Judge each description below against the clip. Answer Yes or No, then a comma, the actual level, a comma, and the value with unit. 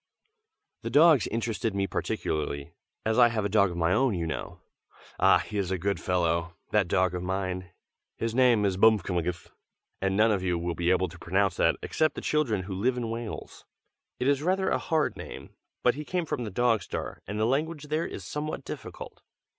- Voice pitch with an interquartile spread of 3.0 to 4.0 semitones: No, average, 5.2 semitones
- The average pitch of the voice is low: Yes, low, 105 Hz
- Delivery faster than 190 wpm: Yes, average, 200 wpm